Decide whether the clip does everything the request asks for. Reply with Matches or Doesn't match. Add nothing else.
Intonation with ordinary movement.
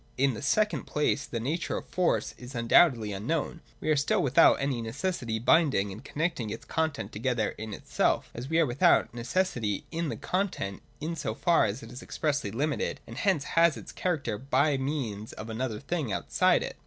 Doesn't match